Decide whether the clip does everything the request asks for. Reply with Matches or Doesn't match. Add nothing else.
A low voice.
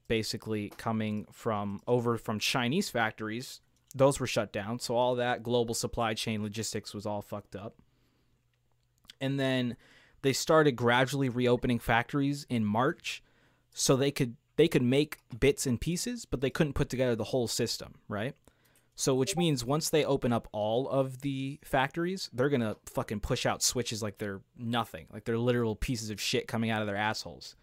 Matches